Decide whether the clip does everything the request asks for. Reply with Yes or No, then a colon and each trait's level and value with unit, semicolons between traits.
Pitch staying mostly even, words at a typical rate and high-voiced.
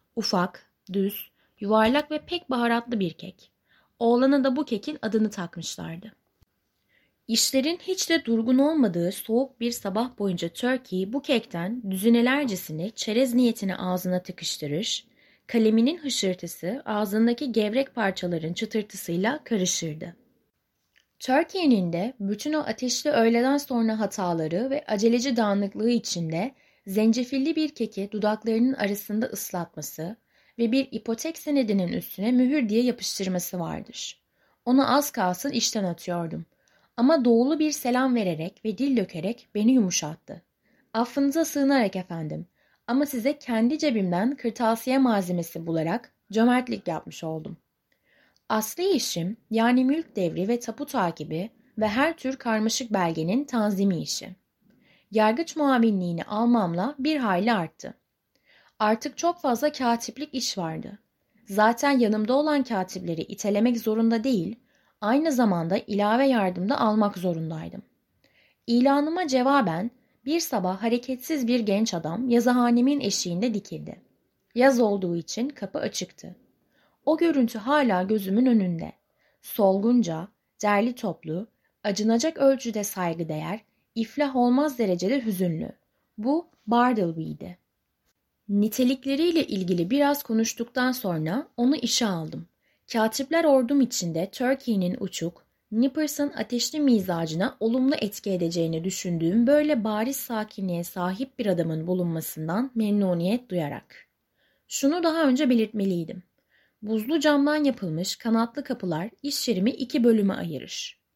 No: wide, 5.5 semitones; average, 115 wpm; high, 225 Hz